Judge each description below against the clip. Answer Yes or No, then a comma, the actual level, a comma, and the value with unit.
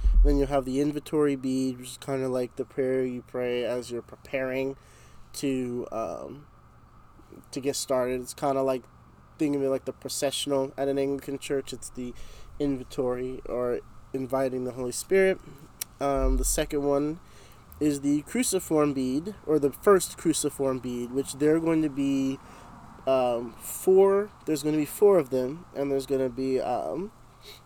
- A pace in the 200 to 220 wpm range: No, average, 165 wpm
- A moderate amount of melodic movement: No, narrow, 2.3 semitones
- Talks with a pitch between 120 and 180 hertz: Yes, low, 135 Hz